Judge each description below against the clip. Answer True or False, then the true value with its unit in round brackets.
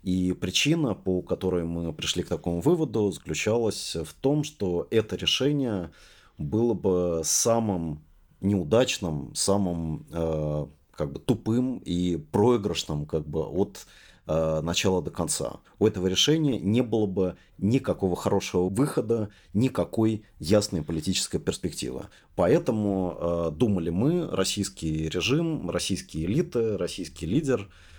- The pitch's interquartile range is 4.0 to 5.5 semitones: True (4.8 semitones)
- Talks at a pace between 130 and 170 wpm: False (120 wpm)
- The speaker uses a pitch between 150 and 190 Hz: False (95 Hz)